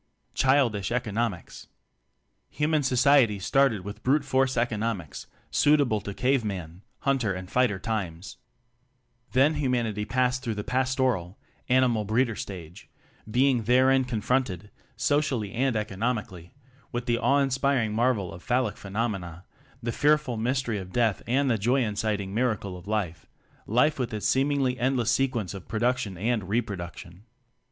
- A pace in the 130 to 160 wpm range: Yes, average, 140 wpm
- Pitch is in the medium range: No, low, 115 Hz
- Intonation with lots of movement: No, average, 4.2 semitones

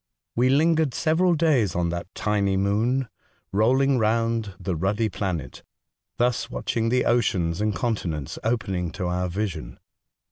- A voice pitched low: Yes, low, 110 Hz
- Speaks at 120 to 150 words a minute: Yes, slow, 135 wpm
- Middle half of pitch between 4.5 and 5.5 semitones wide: Yes, average, 5.0 semitones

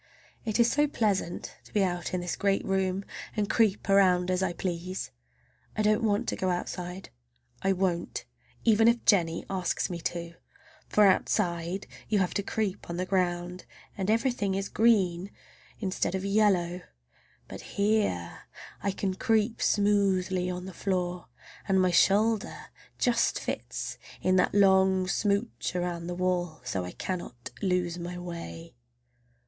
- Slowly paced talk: No, average, 150 wpm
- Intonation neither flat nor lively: No, narrow, 2.3 semitones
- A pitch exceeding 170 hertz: Yes, high, 190 Hz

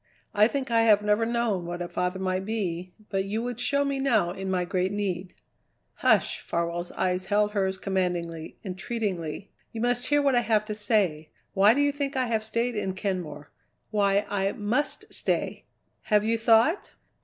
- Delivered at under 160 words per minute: No, average, 180 wpm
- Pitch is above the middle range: Yes, high, 205 Hz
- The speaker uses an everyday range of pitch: Yes, average, 3.8 semitones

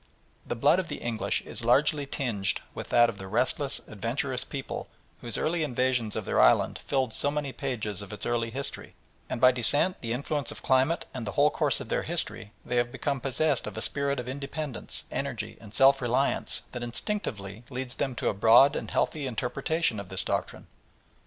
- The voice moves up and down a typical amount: Yes, average, 3.5 semitones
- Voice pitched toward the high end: No, low, 130 Hz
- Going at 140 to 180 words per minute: No, average, 195 wpm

